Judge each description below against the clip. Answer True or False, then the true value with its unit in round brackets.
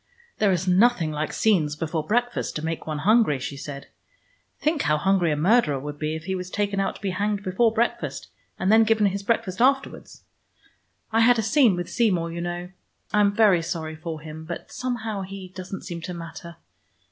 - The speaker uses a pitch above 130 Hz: True (185 Hz)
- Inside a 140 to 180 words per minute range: False (200 wpm)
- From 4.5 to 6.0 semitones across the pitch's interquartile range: True (5.0 semitones)